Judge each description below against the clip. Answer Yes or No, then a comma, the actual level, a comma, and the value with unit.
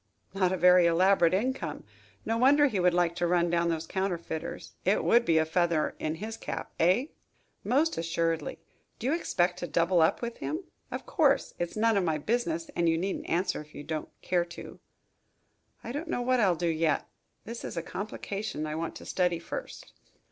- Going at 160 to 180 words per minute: No, average, 195 wpm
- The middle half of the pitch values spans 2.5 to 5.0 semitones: No, wide, 5.4 semitones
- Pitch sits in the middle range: Yes, medium, 180 Hz